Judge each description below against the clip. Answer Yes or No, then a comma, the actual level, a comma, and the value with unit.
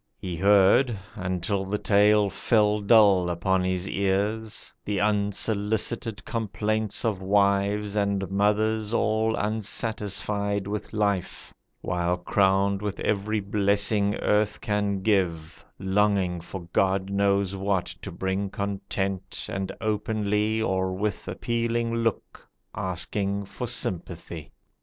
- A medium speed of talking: No, slow, 110 wpm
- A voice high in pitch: No, low, 100 Hz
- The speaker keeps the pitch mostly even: Yes, narrow, 1.8 semitones